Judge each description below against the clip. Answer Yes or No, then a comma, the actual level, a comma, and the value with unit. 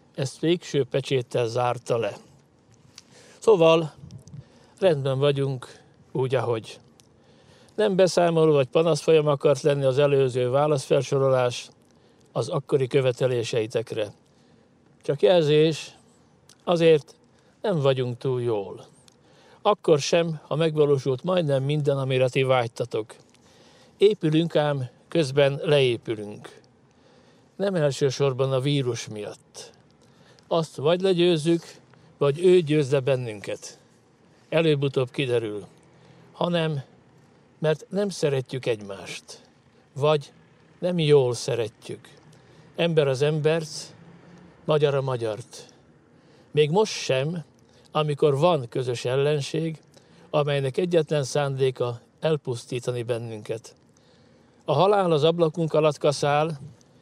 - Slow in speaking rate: Yes, slow, 95 wpm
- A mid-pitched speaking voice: Yes, medium, 145 Hz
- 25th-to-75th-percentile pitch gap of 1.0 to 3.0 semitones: No, average, 3.5 semitones